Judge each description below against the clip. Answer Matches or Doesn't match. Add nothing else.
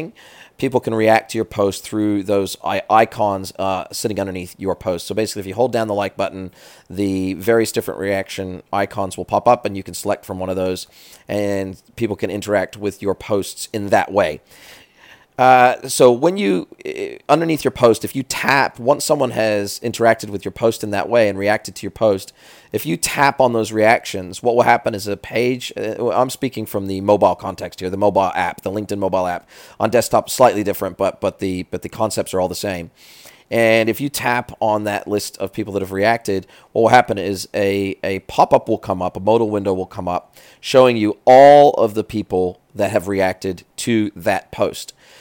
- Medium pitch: Doesn't match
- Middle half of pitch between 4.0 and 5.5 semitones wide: Doesn't match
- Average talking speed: Doesn't match